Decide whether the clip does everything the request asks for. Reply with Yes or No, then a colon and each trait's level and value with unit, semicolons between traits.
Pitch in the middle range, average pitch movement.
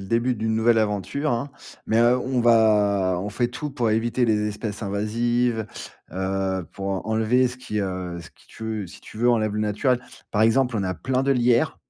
No: low, 110 Hz; average, 3.0 semitones